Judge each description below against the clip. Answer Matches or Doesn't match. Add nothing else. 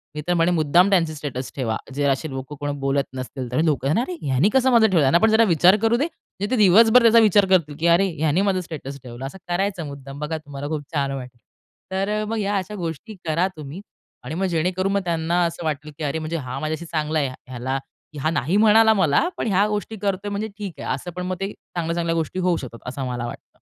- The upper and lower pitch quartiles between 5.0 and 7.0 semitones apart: Matches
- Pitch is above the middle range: Doesn't match